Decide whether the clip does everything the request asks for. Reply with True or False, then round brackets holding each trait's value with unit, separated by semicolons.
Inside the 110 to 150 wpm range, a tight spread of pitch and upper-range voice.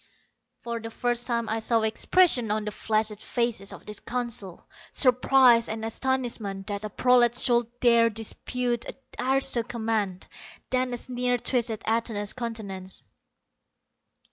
True (135 wpm; 2.2 semitones; 230 Hz)